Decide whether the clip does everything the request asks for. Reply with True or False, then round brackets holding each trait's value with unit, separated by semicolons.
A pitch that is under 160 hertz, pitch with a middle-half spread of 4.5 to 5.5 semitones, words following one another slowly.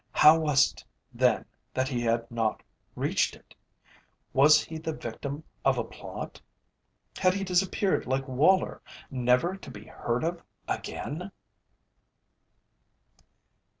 True (140 Hz; 4.9 semitones; 120 wpm)